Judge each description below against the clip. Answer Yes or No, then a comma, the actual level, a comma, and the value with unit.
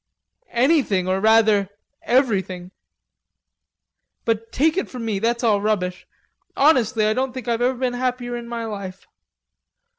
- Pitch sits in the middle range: No, high, 230 Hz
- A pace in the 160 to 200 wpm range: No, average, 140 wpm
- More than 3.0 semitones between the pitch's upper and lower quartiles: Yes, average, 3.4 semitones